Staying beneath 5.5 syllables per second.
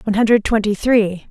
No: 5.9 syllables/s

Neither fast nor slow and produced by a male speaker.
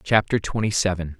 Yes: average, 150 wpm; male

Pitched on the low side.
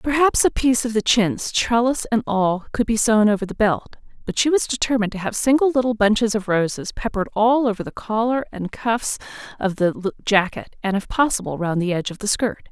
No: high, 220 Hz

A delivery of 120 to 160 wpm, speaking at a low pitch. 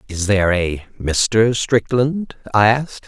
Yes: slow, 135 wpm; low, 110 Hz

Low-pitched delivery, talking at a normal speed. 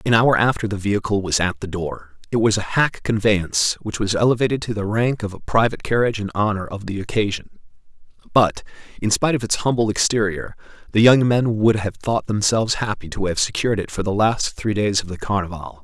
No: low, 105 Hz; fast, 210 wpm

